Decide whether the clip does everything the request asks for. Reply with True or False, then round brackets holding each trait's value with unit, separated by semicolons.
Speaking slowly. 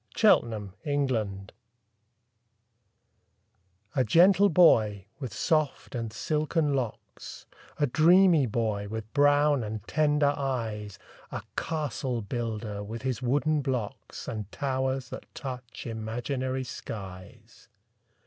True (105 wpm)